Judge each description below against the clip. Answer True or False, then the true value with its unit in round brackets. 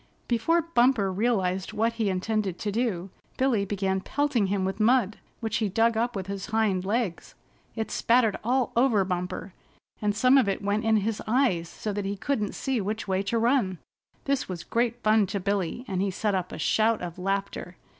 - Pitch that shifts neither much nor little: True (3.4 semitones)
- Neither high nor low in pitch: False (210 Hz)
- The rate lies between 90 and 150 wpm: False (195 wpm)